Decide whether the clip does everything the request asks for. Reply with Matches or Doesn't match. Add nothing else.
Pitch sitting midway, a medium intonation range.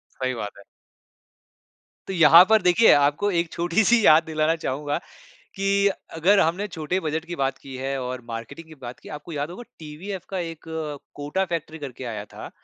Matches